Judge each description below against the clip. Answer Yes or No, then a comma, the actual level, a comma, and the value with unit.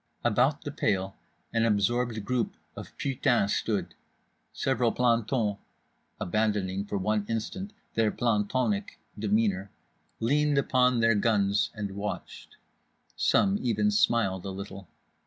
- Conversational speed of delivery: No, slow, 115 wpm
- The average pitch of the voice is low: Yes, low, 110 Hz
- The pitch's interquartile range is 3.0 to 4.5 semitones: Yes, average, 3.3 semitones